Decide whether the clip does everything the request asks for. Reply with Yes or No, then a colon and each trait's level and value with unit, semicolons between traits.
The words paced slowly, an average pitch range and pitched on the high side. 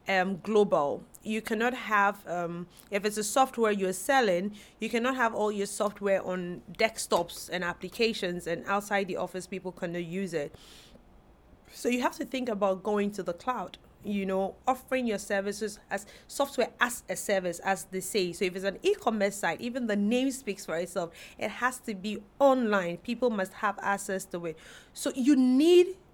No: average, 180 wpm; average, 4.1 semitones; high, 205 Hz